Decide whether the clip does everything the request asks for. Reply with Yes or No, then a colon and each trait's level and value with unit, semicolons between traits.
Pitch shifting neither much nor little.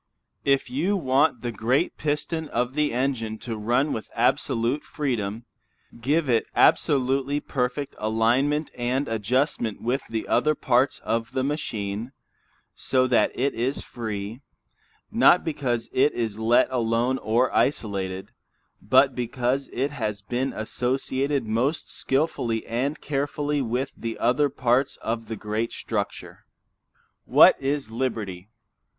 Yes: average, 3.5 semitones